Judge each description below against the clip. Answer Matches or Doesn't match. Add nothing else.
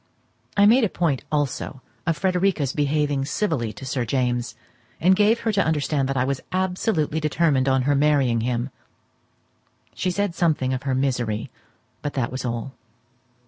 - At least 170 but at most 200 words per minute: Doesn't match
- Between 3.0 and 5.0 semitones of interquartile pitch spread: Matches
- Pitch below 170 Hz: Matches